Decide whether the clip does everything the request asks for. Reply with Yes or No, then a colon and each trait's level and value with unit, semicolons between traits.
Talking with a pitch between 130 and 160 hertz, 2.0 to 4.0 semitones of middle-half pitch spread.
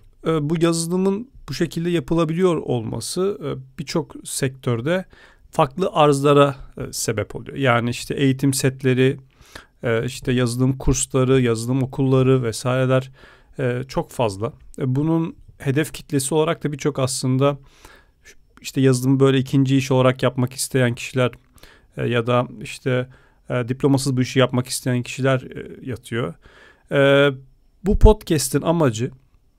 Yes: low, 135 Hz; average, 2.8 semitones